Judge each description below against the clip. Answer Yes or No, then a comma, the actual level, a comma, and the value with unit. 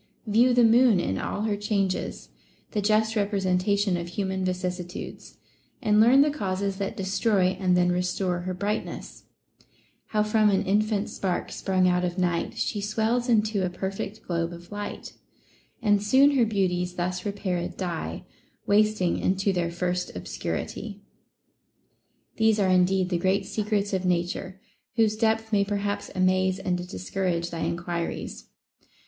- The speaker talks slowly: No, average, 145 wpm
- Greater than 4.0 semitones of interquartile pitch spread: No, average, 2.8 semitones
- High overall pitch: Yes, high, 195 Hz